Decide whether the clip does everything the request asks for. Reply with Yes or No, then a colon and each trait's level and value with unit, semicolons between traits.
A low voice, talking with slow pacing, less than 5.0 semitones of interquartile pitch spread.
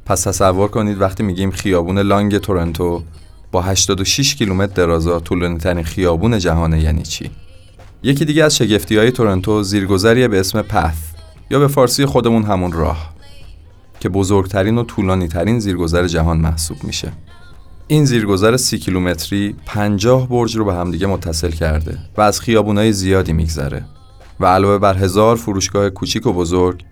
No: very low, 95 Hz; average, 150 wpm; average, 3.6 semitones